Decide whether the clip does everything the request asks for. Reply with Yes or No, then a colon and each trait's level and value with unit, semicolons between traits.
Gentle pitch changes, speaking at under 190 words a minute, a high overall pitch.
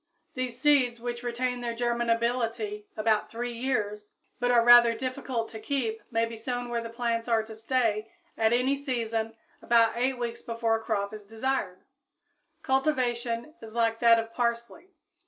Yes: narrow, 1.5 semitones; average, 160 wpm; high, 235 Hz